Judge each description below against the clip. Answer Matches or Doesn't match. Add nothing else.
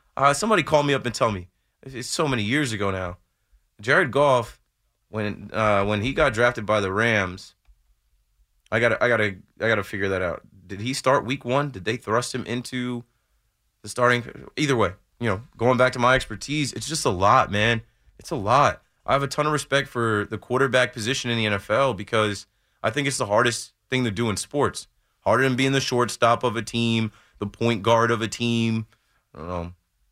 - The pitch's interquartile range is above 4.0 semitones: Doesn't match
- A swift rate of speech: Matches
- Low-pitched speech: Matches